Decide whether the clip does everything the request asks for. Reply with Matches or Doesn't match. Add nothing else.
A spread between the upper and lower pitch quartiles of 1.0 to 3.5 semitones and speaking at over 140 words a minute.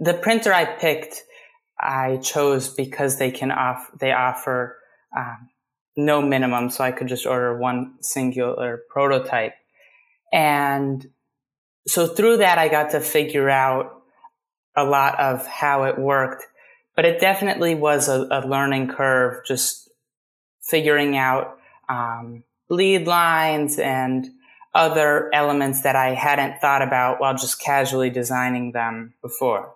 Doesn't match